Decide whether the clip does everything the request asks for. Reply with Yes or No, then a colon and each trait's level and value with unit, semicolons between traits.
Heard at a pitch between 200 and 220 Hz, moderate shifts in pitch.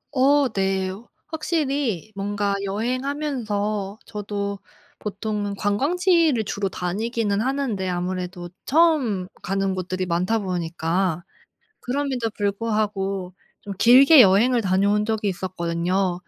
Yes: high, 205 Hz; average, 4.6 semitones